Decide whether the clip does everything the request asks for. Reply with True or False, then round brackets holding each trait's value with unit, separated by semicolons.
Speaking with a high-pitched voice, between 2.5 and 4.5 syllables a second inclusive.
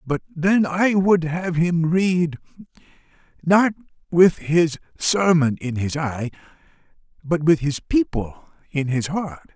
False (165 Hz; 3.5 syllables/s)